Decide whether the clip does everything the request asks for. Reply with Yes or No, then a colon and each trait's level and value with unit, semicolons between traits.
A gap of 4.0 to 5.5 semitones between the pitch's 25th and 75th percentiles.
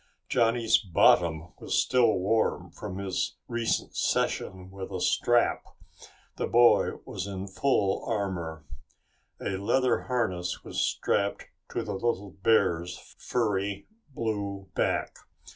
No: average, 3.4 semitones